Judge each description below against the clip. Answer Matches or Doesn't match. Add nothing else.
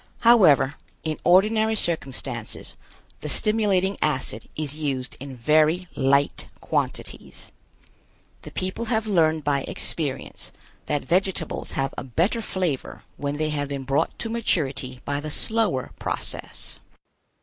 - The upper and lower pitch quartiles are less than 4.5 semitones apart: Doesn't match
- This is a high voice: Doesn't match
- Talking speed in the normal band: Doesn't match